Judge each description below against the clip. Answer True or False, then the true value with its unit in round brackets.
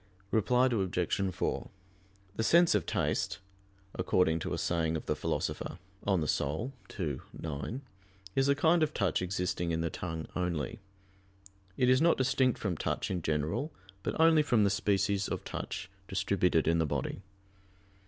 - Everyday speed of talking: True (155 wpm)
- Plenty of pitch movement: True (7.3 semitones)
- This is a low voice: True (95 Hz)